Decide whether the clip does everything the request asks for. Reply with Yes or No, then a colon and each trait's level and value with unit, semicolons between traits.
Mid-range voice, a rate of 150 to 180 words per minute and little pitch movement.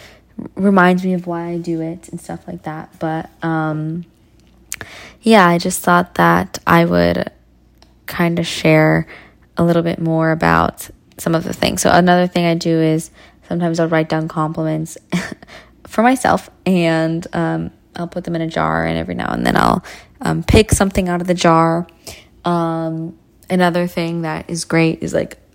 Yes: medium, 165 Hz; average, 175 wpm; narrow, 1.9 semitones